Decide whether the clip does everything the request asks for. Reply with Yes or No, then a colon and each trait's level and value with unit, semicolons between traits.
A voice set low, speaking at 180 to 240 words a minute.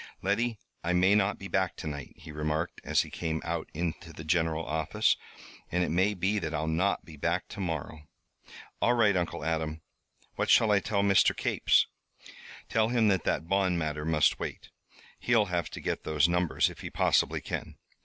Yes: very low, 85 Hz; average, 190 wpm